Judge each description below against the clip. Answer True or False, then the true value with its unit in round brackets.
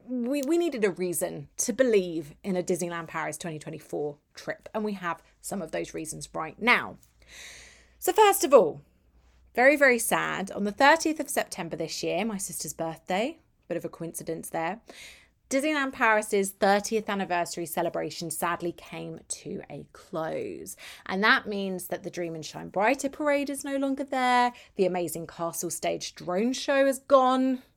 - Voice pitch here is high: True (195 Hz)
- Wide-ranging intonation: True (7.5 semitones)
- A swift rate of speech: False (165 wpm)